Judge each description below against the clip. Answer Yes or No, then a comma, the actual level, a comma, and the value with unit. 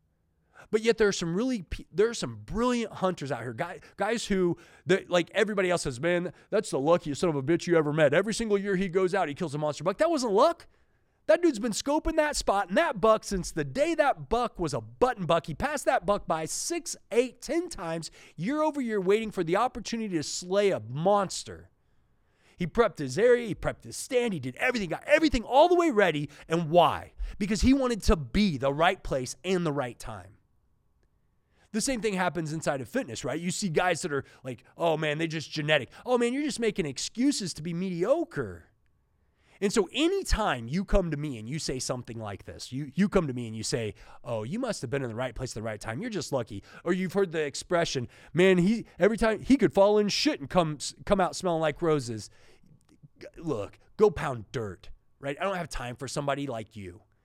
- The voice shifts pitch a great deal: Yes, wide, 7.6 semitones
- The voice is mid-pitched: Yes, medium, 175 Hz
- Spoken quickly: Yes, fast, 225 wpm